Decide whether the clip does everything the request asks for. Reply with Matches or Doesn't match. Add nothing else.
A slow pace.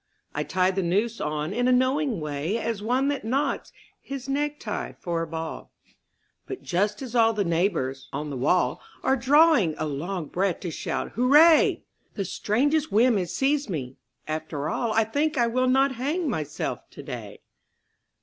Doesn't match